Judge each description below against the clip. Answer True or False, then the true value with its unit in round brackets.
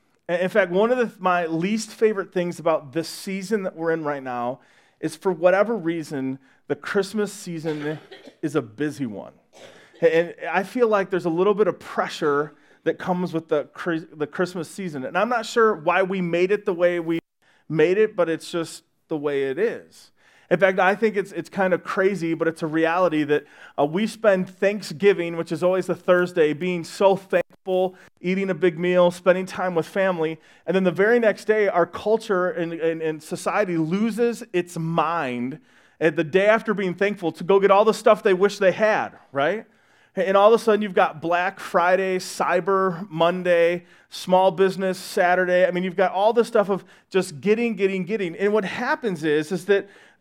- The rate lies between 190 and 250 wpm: True (195 wpm)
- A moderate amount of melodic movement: True (3.2 semitones)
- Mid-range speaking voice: True (180 Hz)